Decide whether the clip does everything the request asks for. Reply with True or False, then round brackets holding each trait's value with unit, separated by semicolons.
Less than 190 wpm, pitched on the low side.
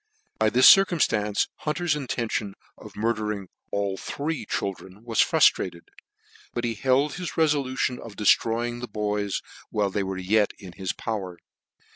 True (150 wpm; 110 Hz)